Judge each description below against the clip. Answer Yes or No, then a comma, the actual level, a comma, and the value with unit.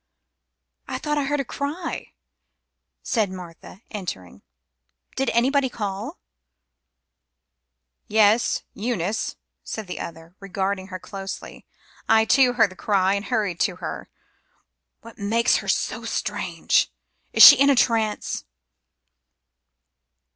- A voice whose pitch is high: Yes, high, 215 Hz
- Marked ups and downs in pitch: No, average, 4.3 semitones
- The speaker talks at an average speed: No, slow, 115 wpm